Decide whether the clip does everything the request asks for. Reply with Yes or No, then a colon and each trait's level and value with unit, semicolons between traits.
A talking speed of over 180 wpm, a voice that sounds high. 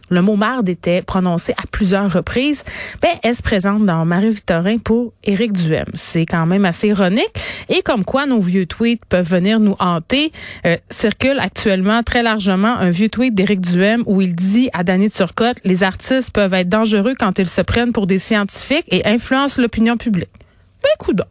Yes: average, 190 wpm; high, 205 Hz